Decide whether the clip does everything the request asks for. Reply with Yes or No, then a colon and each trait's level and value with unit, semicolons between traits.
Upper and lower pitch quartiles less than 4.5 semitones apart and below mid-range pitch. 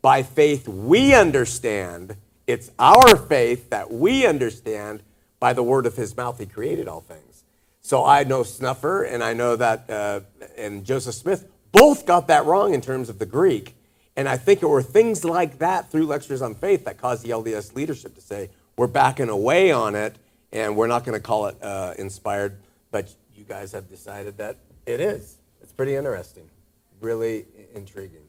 No: average, 4.8 semitones; low, 115 Hz